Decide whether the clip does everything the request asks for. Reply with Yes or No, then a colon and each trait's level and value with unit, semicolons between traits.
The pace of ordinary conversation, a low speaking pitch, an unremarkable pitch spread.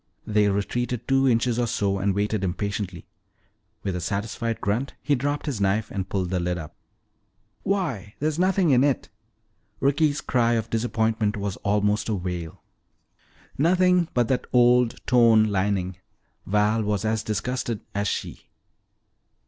Yes: average, 145 wpm; low, 110 Hz; average, 3.7 semitones